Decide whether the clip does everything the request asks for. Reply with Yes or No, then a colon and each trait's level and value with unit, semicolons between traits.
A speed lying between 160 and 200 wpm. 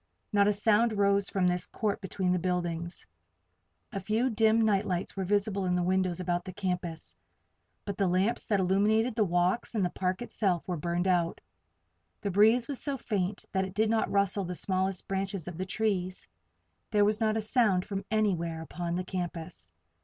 Yes: average, 190 wpm